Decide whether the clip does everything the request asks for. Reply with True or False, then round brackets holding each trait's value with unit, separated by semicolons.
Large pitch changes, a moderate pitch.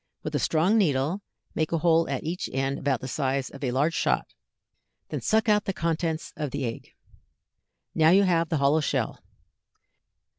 False (3.7 semitones; 160 Hz)